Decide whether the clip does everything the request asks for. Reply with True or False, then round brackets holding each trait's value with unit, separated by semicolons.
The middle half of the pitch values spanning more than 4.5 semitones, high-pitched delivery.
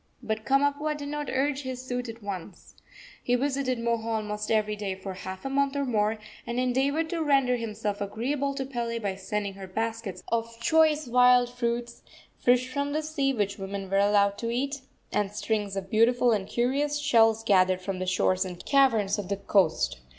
True (4.9 semitones; 230 Hz)